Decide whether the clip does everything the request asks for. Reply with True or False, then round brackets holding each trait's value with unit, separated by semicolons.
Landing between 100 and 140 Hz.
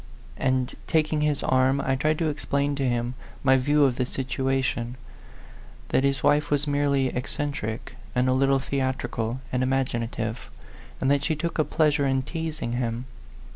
True (135 Hz)